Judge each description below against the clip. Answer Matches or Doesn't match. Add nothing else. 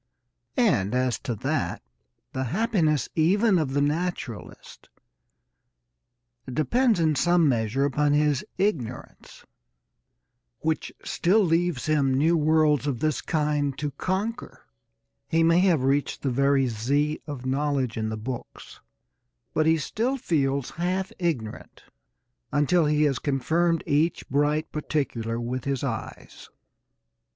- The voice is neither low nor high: Matches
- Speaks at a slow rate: Matches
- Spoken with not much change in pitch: Doesn't match